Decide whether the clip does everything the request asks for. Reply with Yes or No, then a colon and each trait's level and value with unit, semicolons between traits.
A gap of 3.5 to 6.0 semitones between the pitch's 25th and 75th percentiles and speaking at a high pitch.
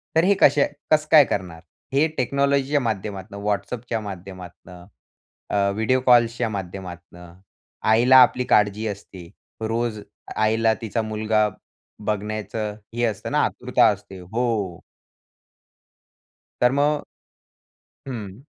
No: average, 3.8 semitones; low, 110 Hz